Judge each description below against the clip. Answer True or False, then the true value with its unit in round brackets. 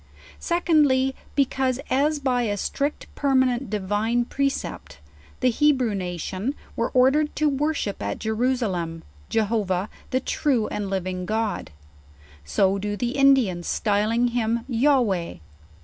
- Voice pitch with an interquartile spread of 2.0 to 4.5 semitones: False (4.9 semitones)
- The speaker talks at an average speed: False (120 wpm)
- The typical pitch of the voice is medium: False (235 Hz)